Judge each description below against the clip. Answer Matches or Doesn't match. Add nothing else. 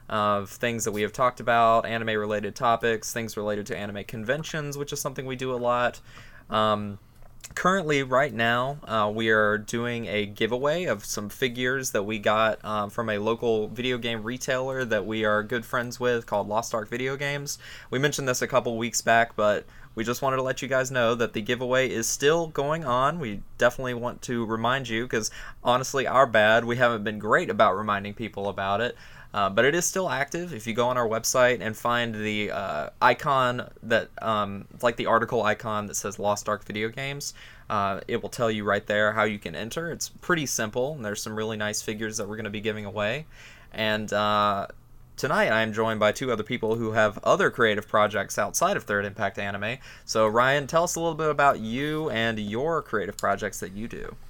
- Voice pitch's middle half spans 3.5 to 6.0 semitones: Doesn't match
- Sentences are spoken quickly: Matches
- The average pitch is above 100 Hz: Matches